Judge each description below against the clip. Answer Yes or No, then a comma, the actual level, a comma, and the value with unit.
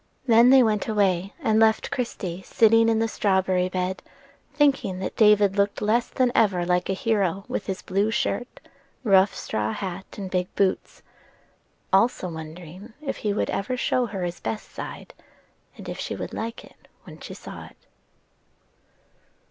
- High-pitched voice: Yes, high, 200 Hz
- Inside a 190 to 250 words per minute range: No, average, 165 wpm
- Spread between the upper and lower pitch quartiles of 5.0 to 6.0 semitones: No, average, 3.4 semitones